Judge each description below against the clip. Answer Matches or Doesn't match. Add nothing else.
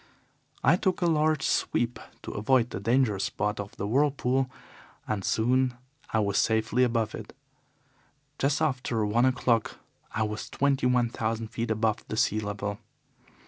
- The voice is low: Matches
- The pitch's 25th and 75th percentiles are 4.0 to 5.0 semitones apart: Doesn't match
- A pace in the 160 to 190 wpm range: Doesn't match